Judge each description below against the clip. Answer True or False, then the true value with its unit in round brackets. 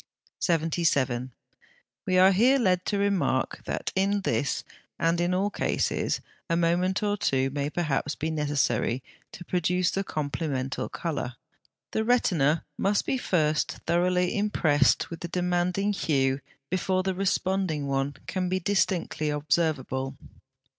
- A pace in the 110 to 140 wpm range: True (135 wpm)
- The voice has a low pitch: False (170 Hz)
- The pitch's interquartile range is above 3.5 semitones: True (4.4 semitones)